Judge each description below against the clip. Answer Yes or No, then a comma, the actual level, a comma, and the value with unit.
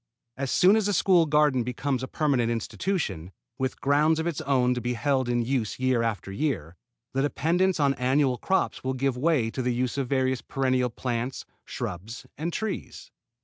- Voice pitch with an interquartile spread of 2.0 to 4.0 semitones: Yes, average, 3.5 semitones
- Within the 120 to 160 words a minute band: No, average, 185 wpm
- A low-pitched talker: Yes, low, 130 Hz